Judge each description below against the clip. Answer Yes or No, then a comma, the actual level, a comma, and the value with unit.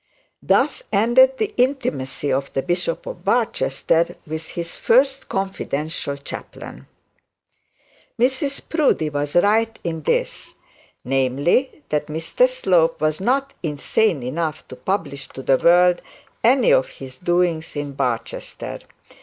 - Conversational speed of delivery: No, slow, 120 wpm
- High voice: No, medium, 170 Hz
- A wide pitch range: Yes, wide, 7.8 semitones